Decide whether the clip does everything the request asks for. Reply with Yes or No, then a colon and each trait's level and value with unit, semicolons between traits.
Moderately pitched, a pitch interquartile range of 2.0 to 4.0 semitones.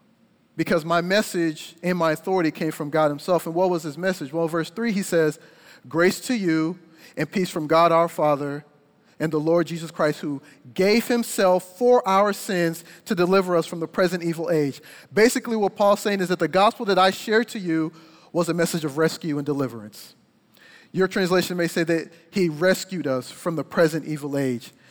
Yes: medium, 170 Hz; average, 3.0 semitones